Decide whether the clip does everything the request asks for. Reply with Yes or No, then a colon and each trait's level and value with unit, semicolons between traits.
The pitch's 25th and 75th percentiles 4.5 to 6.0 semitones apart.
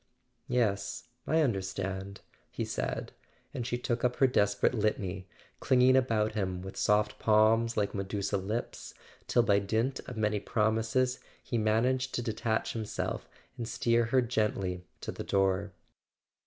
No: average, 3.2 semitones